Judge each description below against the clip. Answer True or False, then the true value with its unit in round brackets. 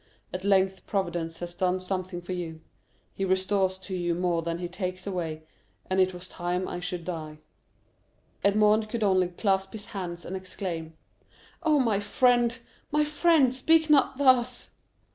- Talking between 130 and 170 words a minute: True (160 wpm)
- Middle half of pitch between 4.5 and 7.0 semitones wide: False (3.3 semitones)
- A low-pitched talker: False (190 Hz)